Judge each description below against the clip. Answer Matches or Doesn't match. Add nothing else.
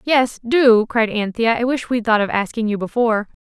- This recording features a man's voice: Doesn't match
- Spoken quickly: Doesn't match